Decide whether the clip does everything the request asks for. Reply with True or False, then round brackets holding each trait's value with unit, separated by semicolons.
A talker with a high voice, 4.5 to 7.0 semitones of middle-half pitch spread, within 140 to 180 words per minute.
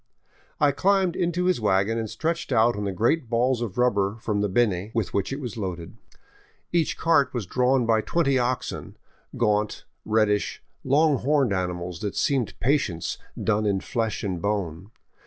False (115 Hz; 5.2 semitones; 165 wpm)